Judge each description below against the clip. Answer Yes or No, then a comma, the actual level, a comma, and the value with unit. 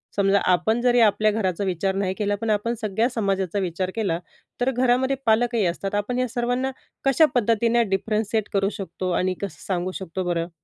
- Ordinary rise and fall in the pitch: Yes, average, 3.6 semitones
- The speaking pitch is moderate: No, high, 205 Hz